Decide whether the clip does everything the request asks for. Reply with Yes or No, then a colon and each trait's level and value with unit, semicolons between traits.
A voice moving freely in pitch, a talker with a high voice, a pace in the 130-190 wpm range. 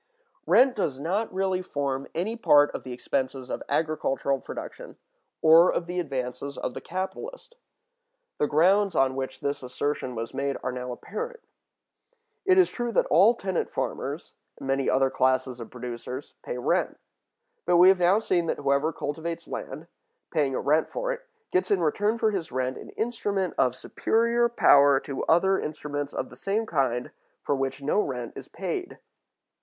No: wide, 6.3 semitones; medium, 155 Hz; average, 170 wpm